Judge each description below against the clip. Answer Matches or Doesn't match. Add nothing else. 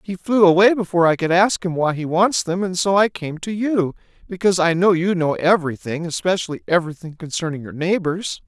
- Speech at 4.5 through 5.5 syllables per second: Doesn't match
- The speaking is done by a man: Matches